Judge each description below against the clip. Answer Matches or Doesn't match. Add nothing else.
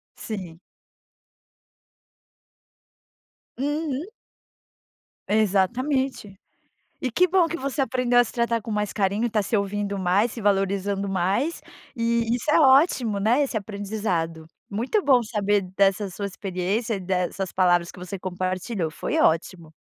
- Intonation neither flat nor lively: Matches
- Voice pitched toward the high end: Matches